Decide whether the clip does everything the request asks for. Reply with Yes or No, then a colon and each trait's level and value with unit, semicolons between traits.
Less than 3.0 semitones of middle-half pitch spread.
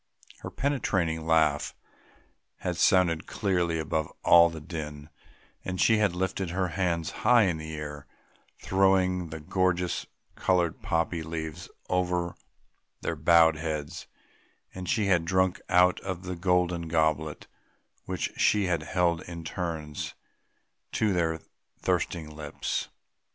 Yes: narrow, 2.5 semitones